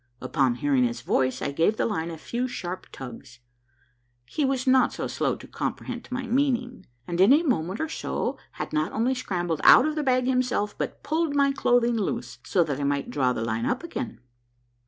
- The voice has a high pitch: Yes, high, 220 Hz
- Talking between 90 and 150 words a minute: No, average, 200 wpm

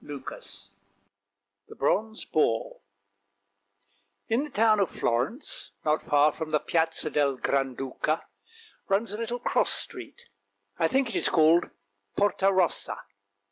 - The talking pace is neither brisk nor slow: No, slow, 130 wpm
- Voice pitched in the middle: Yes, medium, 165 Hz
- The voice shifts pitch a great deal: Yes, wide, 7.1 semitones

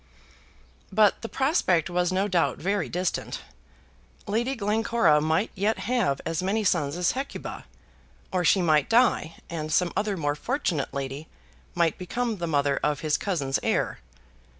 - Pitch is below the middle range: No, medium, 180 Hz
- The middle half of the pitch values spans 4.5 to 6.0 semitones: Yes, wide, 5.5 semitones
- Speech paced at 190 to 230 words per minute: No, average, 150 wpm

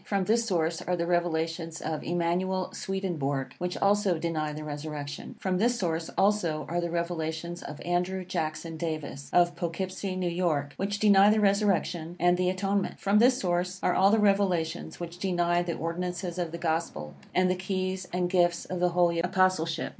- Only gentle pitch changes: Yes, narrow, 2.3 semitones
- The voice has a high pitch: No, medium, 175 Hz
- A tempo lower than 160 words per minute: No, average, 175 wpm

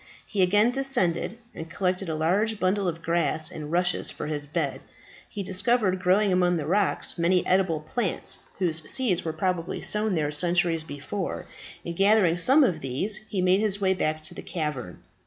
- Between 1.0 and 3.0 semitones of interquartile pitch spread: No, average, 3.8 semitones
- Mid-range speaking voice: Yes, medium, 180 Hz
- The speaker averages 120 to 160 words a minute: No, average, 175 wpm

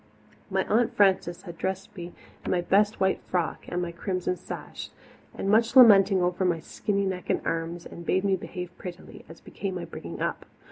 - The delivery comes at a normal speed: Yes, average, 190 wpm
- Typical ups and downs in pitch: No, narrow, 2.1 semitones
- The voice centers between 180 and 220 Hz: Yes, medium, 185 Hz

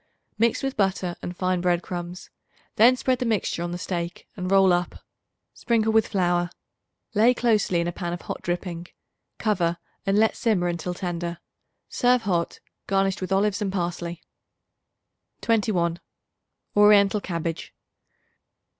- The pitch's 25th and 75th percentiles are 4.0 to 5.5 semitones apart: No, average, 3.3 semitones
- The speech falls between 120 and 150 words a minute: Yes, average, 140 wpm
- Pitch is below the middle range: No, medium, 185 Hz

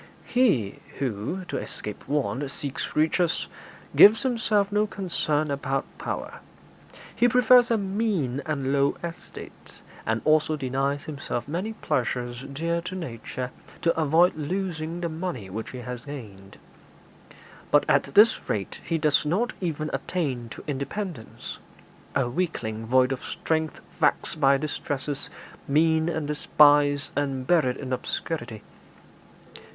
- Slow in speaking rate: Yes, slow, 130 wpm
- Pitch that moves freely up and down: No, average, 4.9 semitones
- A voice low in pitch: No, medium, 150 Hz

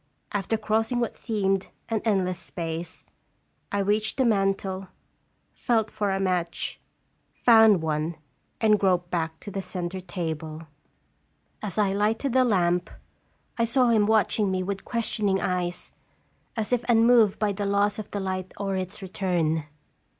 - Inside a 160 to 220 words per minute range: No, average, 150 wpm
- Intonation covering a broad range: No, average, 3.2 semitones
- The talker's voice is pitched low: No, high, 195 Hz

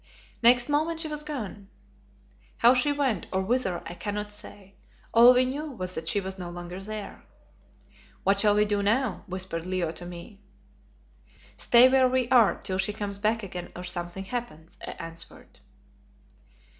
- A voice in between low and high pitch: No, high, 205 Hz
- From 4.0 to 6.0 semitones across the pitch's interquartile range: Yes, average, 5.2 semitones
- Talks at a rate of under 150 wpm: No, average, 165 wpm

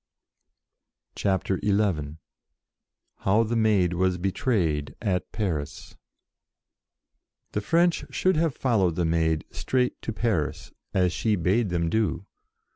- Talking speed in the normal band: No, slow, 115 wpm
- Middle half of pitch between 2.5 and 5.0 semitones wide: Yes, average, 4.7 semitones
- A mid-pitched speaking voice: No, very low, 95 Hz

